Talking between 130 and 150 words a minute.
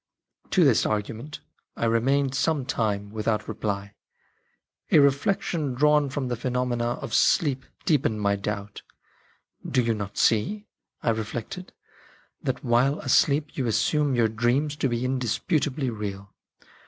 Yes: average, 140 wpm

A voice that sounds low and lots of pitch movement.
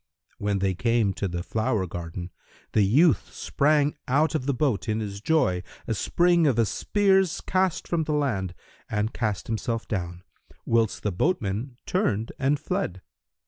Yes: low, 115 Hz; wide, 7.4 semitones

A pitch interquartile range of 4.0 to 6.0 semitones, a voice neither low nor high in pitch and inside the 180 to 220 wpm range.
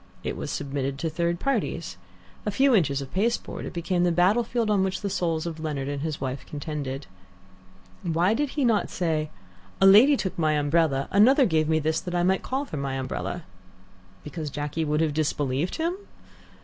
Yes: average, 4.8 semitones; medium, 165 Hz; average, 190 wpm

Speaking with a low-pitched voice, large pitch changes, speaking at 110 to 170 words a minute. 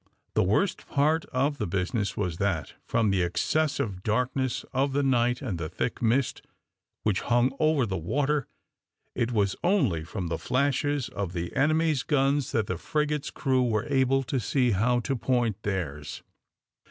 Yes: low, 125 Hz; wide, 5.9 semitones; average, 165 wpm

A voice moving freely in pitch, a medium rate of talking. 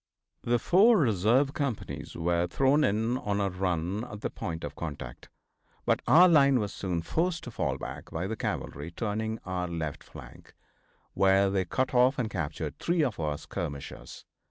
Yes: wide, 7.0 semitones; average, 170 wpm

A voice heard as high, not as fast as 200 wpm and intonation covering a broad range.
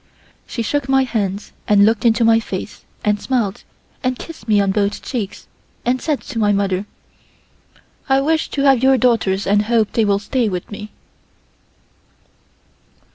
No: high, 225 Hz; average, 160 wpm; average, 4.0 semitones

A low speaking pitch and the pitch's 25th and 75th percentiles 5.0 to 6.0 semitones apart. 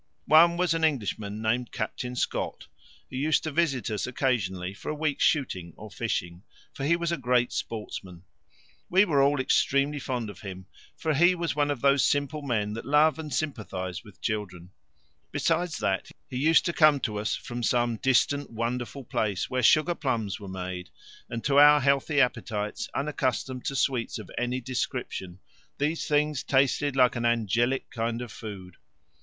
Yes: low, 125 Hz; average, 5.3 semitones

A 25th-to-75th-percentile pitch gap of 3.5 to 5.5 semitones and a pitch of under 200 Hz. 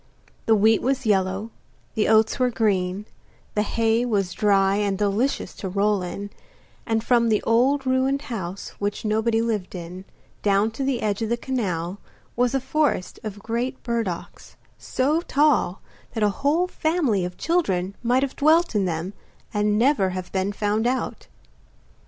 No: average, 4.3 semitones; high, 220 Hz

